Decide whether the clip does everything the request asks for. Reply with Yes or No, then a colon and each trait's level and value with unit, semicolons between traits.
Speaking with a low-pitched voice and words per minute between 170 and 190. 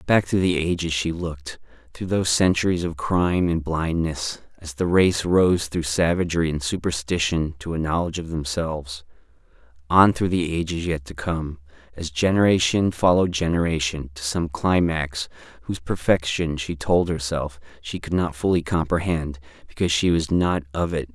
No: very low, 80 Hz; average, 160 wpm